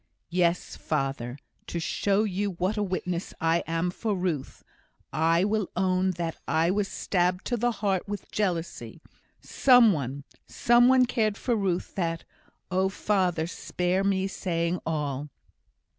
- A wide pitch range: No, average, 3.5 semitones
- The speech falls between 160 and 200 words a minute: No, average, 145 wpm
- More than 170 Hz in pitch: Yes, medium, 185 Hz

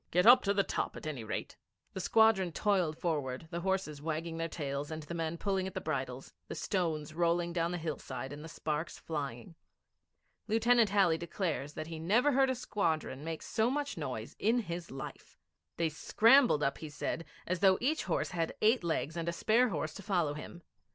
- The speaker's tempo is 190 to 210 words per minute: Yes, average, 200 wpm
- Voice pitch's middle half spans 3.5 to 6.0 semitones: Yes, average, 4.5 semitones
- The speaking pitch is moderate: Yes, medium, 170 Hz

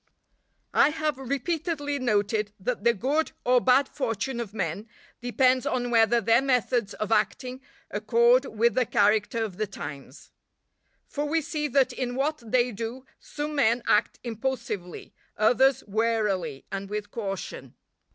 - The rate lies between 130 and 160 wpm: Yes, average, 145 wpm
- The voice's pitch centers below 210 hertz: No, high, 235 Hz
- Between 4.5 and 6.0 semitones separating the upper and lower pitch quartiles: No, average, 3.9 semitones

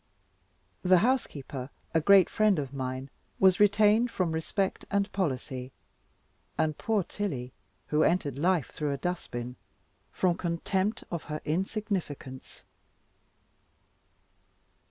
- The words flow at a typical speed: No, slow, 115 wpm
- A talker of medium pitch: Yes, medium, 170 Hz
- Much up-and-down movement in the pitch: Yes, wide, 6.1 semitones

